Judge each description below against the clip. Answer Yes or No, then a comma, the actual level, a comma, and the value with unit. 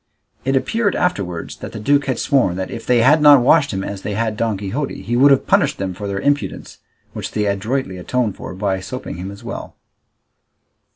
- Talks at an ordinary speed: No, fast, 210 wpm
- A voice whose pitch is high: No, low, 115 Hz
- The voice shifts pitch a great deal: Yes, wide, 5.8 semitones